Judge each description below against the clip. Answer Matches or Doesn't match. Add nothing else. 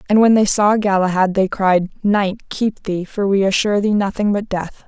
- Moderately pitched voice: Doesn't match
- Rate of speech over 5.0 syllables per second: Doesn't match